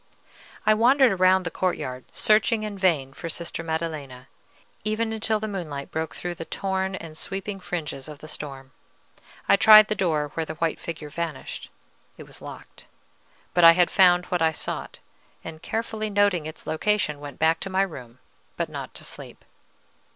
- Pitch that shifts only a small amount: No, average, 4.4 semitones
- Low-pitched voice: No, medium, 175 Hz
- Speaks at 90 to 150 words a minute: No, average, 175 wpm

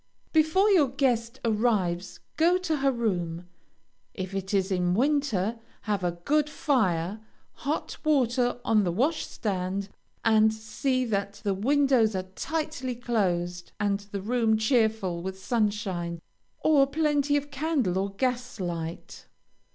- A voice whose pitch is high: Yes, high, 220 Hz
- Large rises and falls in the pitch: Yes, wide, 6.2 semitones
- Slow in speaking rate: Yes, slow, 130 wpm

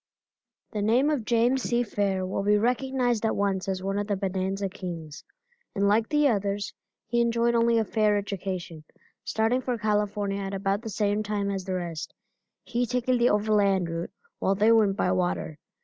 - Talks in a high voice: Yes, high, 205 Hz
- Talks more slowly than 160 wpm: No, average, 180 wpm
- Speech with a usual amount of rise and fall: Yes, average, 3.1 semitones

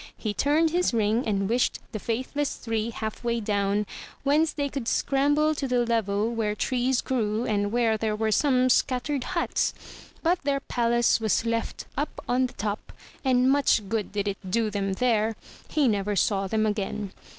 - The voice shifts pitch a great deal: No, average, 3.8 semitones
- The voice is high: Yes, high, 230 Hz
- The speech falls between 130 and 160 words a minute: No, average, 175 wpm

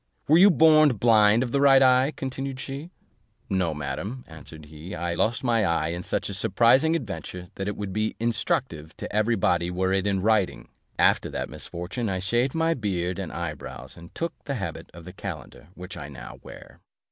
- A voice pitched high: No, low, 100 Hz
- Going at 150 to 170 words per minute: No, average, 195 wpm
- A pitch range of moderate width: No, wide, 6.6 semitones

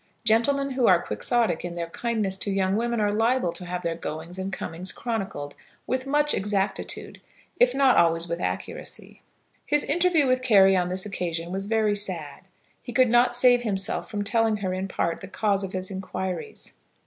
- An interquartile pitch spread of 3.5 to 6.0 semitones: Yes, average, 4.8 semitones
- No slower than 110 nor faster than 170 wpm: No, average, 185 wpm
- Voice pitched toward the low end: No, high, 200 Hz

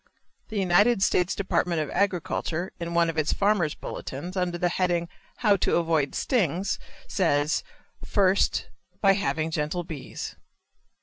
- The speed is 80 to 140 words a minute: Yes, slow, 135 wpm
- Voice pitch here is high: No, medium, 175 Hz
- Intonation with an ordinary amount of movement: Yes, average, 3.1 semitones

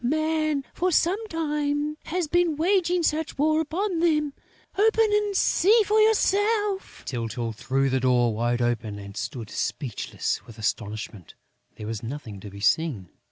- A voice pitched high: Yes, very high, 295 Hz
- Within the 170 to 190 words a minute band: No, average, 150 wpm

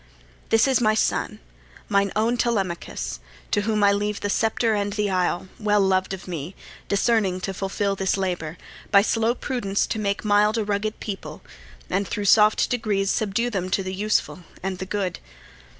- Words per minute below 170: No, average, 175 wpm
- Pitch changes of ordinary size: No, narrow, 2.0 semitones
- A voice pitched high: Yes, high, 200 Hz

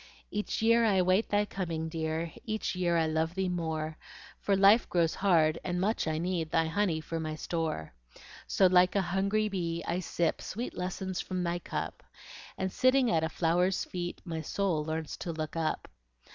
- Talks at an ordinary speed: Yes, average, 185 wpm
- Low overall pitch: No, medium, 175 Hz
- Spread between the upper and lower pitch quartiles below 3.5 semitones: Yes, average, 3.0 semitones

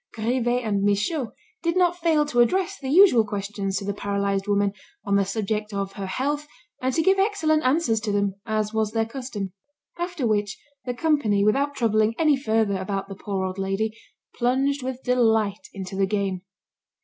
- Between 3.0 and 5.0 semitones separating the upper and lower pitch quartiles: No, wide, 5.4 semitones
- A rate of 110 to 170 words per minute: No, average, 180 wpm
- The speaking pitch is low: No, high, 220 Hz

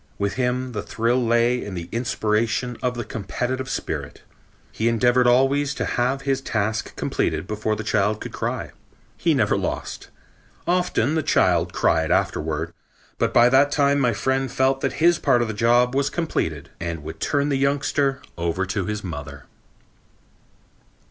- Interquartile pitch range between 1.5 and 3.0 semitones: No, average, 4.1 semitones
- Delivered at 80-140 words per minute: No, average, 170 wpm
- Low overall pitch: Yes, low, 120 Hz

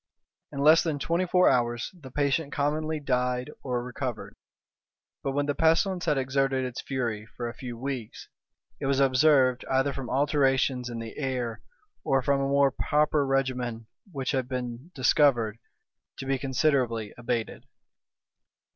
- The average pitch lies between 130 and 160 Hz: Yes, low, 135 Hz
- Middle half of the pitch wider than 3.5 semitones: No, narrow, 2.5 semitones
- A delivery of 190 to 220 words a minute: No, average, 150 wpm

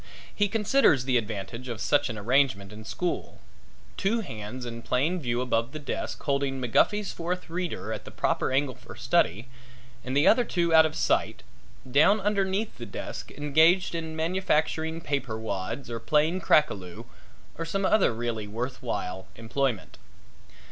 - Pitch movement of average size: No, wide, 6.4 semitones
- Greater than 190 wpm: No, average, 160 wpm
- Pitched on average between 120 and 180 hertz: Yes, medium, 140 Hz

